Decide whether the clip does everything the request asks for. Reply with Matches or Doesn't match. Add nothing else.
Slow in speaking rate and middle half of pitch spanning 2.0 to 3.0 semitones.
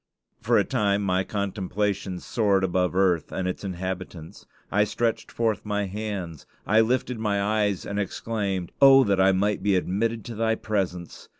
Doesn't match